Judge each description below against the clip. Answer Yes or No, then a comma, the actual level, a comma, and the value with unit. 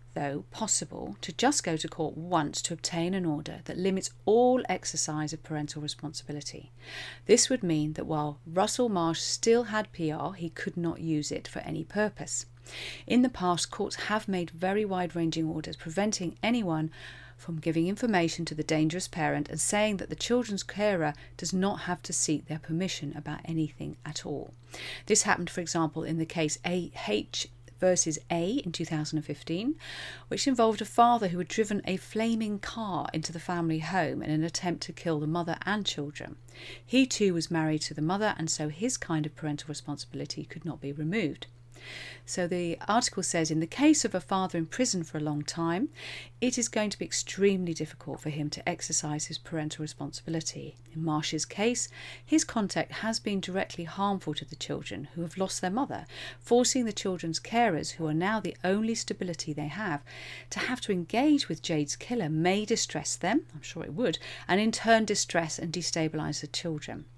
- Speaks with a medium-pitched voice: Yes, medium, 165 Hz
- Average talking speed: Yes, average, 185 wpm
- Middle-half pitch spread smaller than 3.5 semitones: No, average, 4.4 semitones